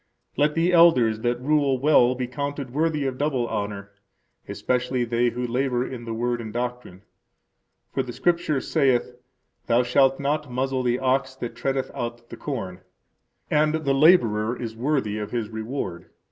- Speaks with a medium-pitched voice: No, low, 125 Hz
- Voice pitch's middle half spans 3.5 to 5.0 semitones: No, average, 3.0 semitones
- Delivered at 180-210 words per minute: No, average, 160 wpm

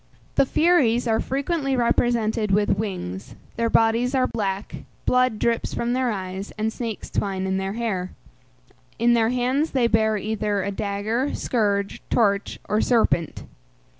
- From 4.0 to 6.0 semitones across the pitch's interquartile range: No, average, 3.3 semitones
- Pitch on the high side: Yes, high, 220 Hz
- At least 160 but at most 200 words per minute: No, average, 145 wpm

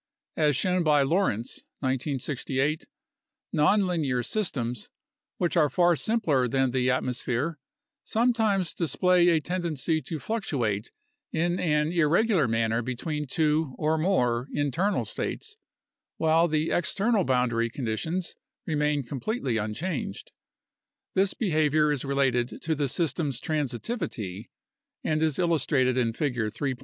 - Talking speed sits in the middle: No, slow, 120 wpm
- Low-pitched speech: No, medium, 150 Hz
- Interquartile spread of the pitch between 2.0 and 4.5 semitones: No, average, 5.2 semitones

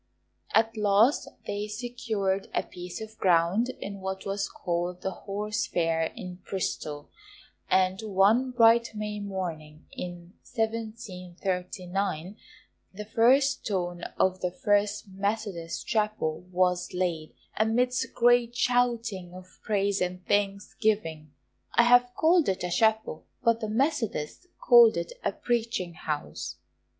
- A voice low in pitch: No, high, 200 Hz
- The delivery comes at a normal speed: No, slow, 120 wpm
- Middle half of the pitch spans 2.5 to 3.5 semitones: No, average, 4.0 semitones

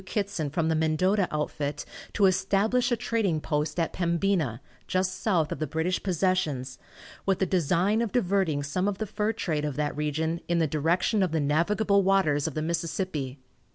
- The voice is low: No, medium, 170 Hz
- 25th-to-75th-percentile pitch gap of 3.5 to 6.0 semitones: Yes, average, 4.3 semitones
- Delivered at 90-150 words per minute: No, average, 180 wpm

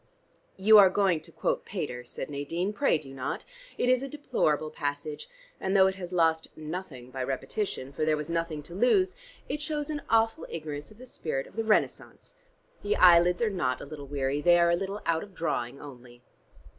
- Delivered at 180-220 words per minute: Yes, average, 200 wpm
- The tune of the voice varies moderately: No, wide, 6.0 semitones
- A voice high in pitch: No, medium, 170 Hz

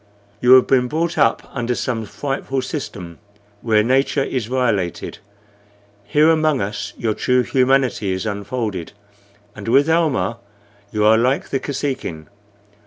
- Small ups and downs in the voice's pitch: No, average, 4.2 semitones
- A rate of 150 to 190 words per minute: No, slow, 135 wpm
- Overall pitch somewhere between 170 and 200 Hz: No, low, 125 Hz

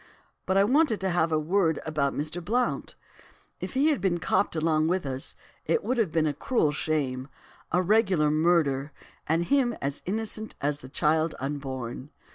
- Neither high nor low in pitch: Yes, medium, 160 Hz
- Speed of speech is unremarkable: Yes, average, 175 wpm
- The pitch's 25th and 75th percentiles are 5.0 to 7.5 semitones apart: Yes, average, 5.3 semitones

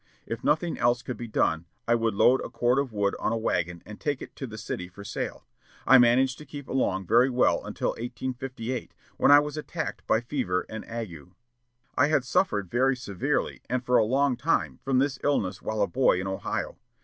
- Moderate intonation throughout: Yes, average, 3.9 semitones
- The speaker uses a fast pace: Yes, fast, 210 wpm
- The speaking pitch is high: No, low, 120 Hz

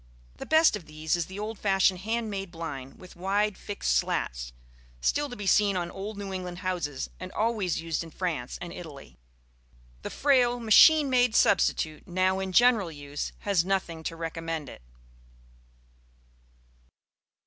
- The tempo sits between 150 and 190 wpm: Yes, average, 155 wpm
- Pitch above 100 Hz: Yes, medium, 185 Hz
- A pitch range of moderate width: Yes, average, 4.2 semitones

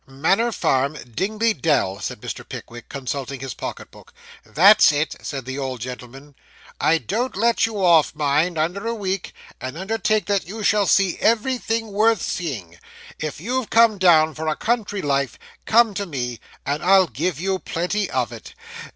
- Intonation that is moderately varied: No, wide, 7.1 semitones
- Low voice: No, medium, 175 Hz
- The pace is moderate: Yes, average, 170 wpm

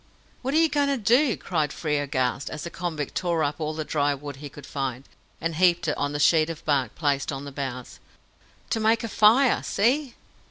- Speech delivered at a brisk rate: Yes, fast, 215 wpm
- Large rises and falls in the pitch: Yes, wide, 7.0 semitones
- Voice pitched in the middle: Yes, medium, 155 Hz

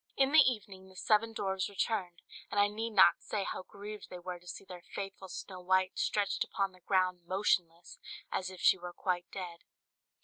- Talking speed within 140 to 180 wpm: No, average, 200 wpm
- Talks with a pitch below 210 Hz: Yes, high, 190 Hz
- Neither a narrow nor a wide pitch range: No, narrow, 2.2 semitones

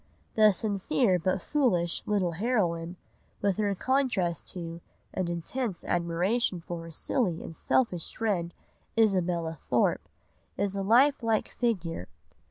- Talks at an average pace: No, slow, 125 wpm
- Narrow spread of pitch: No, average, 4.6 semitones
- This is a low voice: No, medium, 185 Hz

